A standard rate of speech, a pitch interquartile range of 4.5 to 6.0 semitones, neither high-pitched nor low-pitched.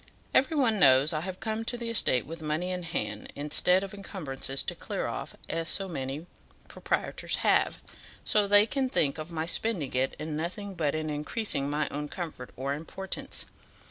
Yes: average, 180 wpm; average, 5.2 semitones; medium, 165 Hz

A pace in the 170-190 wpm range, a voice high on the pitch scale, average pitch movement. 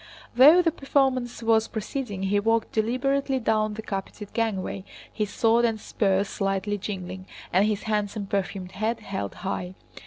No: average, 150 wpm; high, 215 Hz; average, 3.0 semitones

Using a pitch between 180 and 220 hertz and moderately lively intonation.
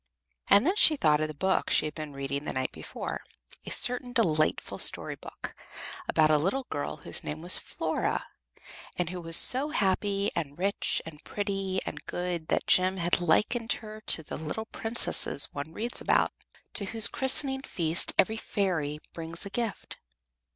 No: medium, 185 Hz; wide, 5.9 semitones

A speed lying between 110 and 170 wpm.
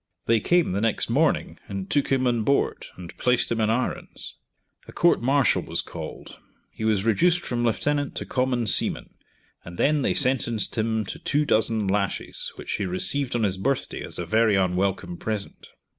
No: average, 180 wpm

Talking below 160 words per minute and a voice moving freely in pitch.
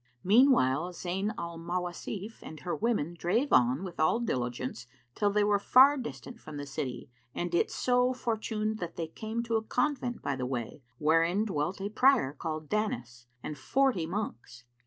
No: average, 170 wpm; wide, 6.9 semitones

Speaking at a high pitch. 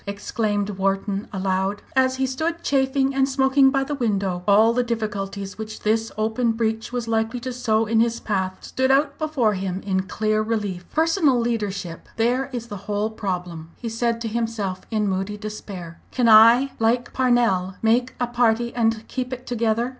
Yes: high, 225 Hz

